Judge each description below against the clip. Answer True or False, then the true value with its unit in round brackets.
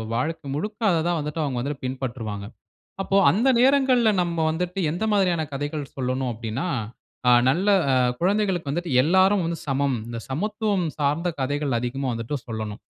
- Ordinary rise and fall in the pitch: False (6.1 semitones)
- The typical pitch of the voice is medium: True (155 Hz)